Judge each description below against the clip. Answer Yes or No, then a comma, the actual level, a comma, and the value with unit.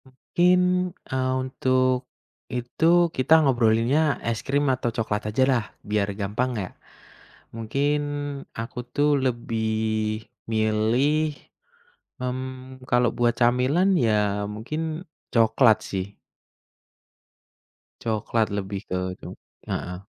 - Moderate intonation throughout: Yes, average, 3.2 semitones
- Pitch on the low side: Yes, low, 120 Hz